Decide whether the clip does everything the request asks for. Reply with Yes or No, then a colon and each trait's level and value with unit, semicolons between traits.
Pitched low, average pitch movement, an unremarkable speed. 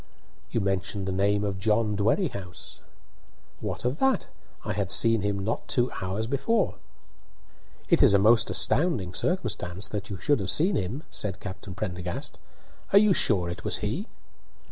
Yes: low, 105 Hz; average, 4.2 semitones; average, 160 wpm